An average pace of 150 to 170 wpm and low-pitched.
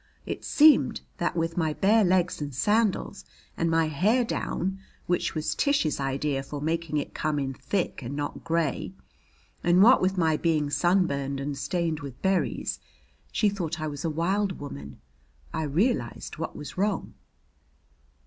No: average, 160 wpm; medium, 165 Hz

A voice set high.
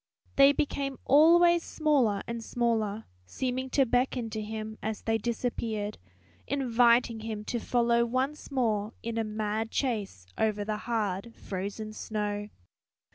Yes: high, 230 Hz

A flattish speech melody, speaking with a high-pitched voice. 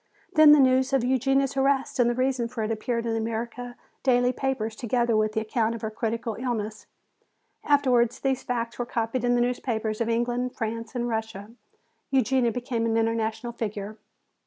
Yes: narrow, 2.2 semitones; high, 235 Hz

